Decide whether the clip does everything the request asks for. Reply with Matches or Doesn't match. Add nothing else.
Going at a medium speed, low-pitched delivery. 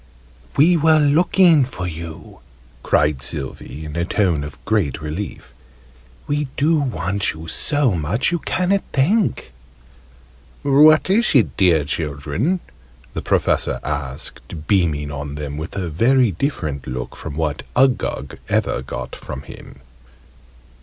Doesn't match